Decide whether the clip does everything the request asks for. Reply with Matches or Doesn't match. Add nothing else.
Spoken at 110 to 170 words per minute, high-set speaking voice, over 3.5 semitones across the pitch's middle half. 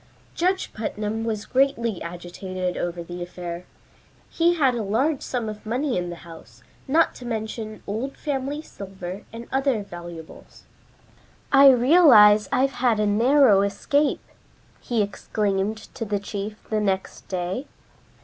Matches